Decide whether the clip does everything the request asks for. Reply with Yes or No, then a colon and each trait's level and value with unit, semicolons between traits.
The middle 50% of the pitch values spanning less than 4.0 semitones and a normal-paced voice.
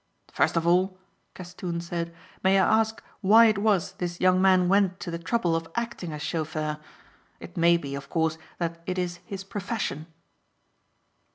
Yes: narrow, 2.5 semitones; average, 170 wpm